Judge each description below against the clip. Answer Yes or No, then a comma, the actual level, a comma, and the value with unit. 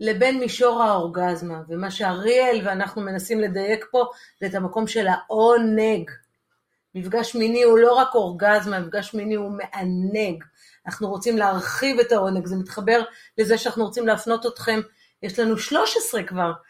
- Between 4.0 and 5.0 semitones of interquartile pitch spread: No, average, 3.2 semitones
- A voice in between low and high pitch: No, high, 215 Hz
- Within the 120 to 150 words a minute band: Yes, average, 145 wpm